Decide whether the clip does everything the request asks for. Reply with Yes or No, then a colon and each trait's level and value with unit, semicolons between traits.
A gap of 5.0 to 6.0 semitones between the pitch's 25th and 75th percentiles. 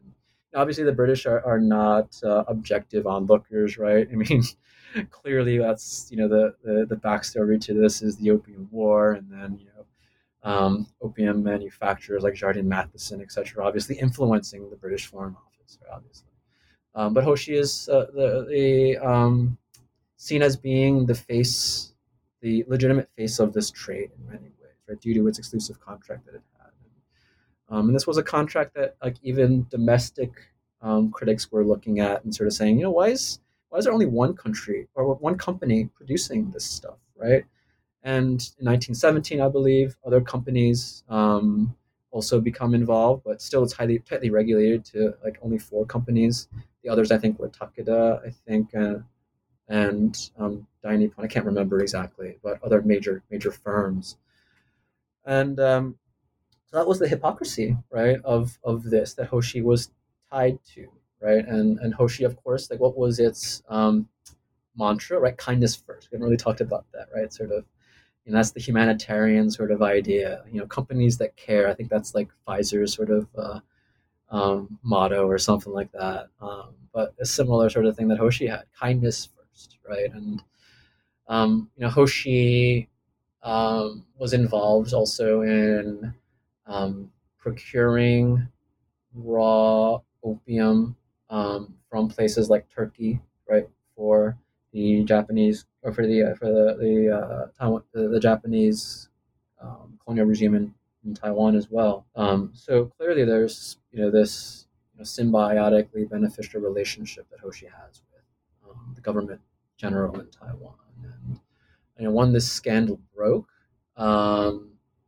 No: narrow, 2.5 semitones